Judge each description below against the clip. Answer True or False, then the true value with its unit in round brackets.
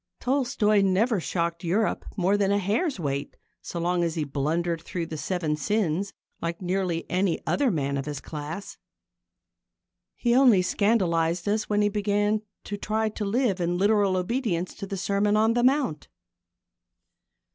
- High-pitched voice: True (195 Hz)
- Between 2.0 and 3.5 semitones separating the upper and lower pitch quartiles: False (4.0 semitones)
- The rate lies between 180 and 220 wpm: False (155 wpm)